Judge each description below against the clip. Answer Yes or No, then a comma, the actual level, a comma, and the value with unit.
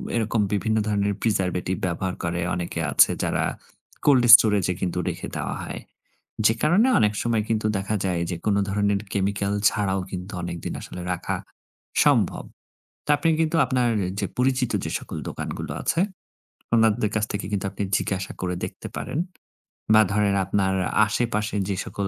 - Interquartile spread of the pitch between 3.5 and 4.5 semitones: No, average, 2.7 semitones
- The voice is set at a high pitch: No, low, 100 Hz